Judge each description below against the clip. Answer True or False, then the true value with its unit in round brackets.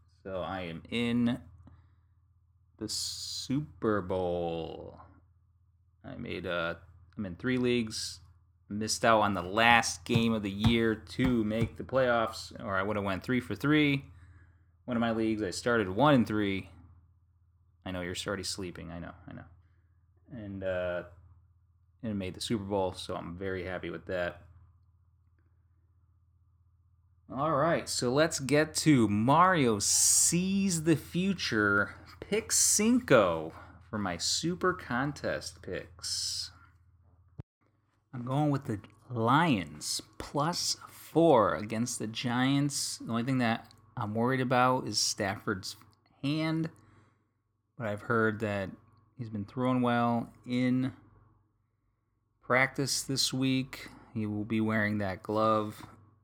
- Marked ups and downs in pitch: False (4.6 semitones)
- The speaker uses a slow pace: True (130 wpm)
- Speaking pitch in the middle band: False (105 Hz)